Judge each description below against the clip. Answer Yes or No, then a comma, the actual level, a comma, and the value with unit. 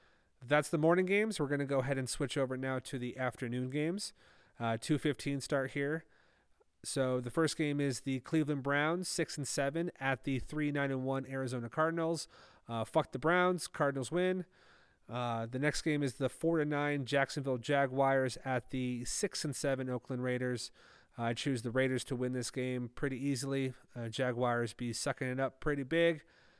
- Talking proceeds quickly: No, average, 180 wpm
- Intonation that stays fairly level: No, average, 3.0 semitones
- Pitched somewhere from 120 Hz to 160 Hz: Yes, low, 135 Hz